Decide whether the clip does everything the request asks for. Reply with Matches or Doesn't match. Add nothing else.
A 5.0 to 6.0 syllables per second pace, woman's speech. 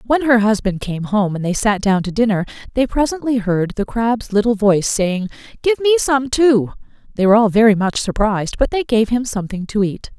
Matches